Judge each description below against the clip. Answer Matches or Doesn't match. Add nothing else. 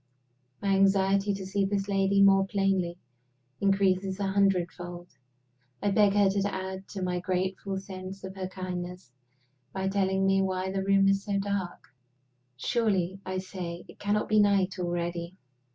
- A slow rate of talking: Doesn't match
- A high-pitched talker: Matches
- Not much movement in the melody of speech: Matches